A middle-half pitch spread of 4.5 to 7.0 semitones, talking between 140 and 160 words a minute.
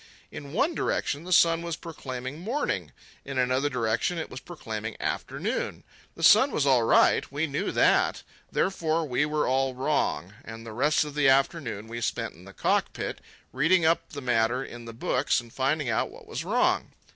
No: average, 5.0 semitones; average, 180 wpm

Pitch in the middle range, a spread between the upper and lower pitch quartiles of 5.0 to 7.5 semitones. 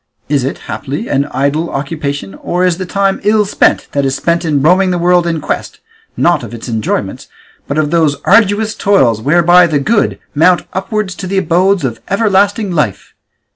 Yes: medium, 170 Hz; average, 5.3 semitones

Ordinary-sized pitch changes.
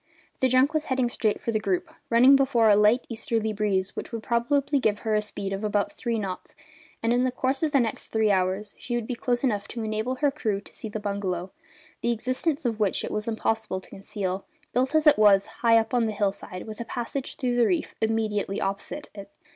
Yes: average, 3.5 semitones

